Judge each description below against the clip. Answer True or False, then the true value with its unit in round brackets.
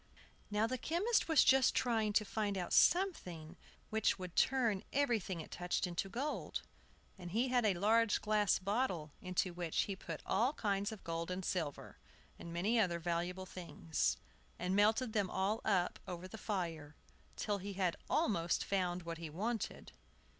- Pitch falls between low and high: False (195 Hz)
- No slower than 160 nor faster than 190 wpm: True (165 wpm)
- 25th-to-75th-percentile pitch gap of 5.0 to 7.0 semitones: False (4.0 semitones)